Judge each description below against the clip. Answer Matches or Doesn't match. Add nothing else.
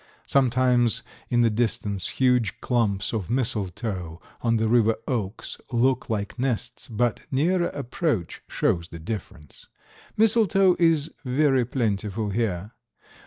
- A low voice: Matches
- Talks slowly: Matches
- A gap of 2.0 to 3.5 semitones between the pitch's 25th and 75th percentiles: Doesn't match